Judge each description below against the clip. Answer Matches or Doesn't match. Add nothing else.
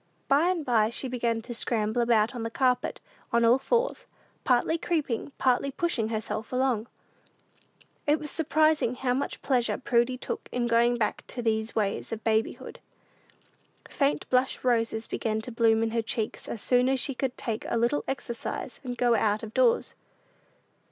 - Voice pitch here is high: Matches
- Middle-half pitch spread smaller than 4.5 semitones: Matches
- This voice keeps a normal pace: Matches